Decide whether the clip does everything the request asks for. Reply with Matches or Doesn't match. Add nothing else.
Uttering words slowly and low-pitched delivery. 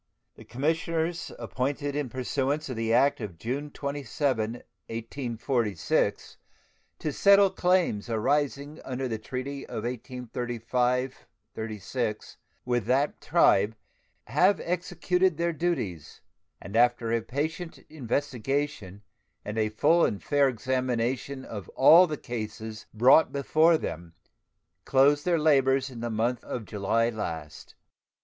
Matches